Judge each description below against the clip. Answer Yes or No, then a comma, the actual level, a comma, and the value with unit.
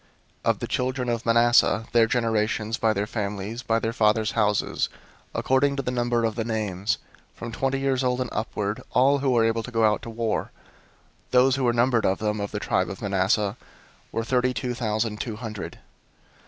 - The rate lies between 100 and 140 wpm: No, average, 200 wpm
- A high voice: No, low, 115 Hz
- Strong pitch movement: No, average, 2.8 semitones